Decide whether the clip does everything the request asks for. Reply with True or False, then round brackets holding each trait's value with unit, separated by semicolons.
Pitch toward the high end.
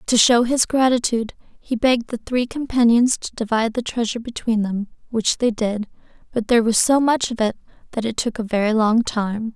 True (230 Hz)